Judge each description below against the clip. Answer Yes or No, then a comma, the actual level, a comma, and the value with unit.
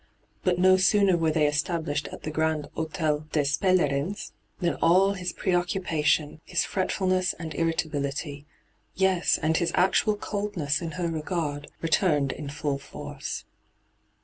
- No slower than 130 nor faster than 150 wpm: Yes, average, 145 wpm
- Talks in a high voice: No, medium, 165 Hz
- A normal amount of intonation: Yes, average, 3.6 semitones